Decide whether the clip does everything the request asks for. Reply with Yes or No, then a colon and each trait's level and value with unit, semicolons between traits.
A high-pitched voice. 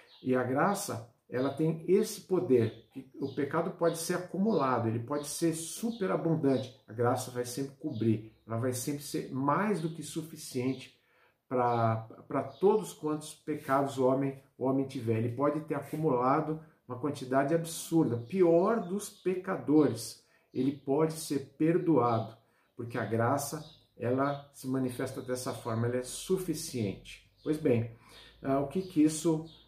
No: medium, 140 Hz